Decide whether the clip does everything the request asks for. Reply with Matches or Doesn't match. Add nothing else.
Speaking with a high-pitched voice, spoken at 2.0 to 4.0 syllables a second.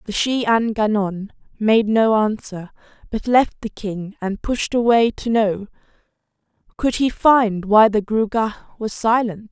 Matches